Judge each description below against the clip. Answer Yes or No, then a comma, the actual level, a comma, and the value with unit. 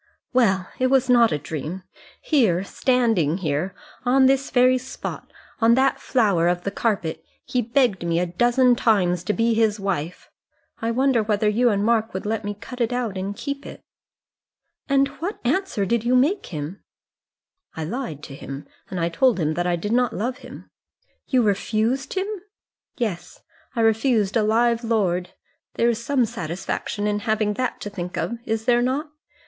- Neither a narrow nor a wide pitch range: Yes, average, 4.8 semitones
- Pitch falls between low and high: No, high, 225 Hz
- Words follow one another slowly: No, average, 175 wpm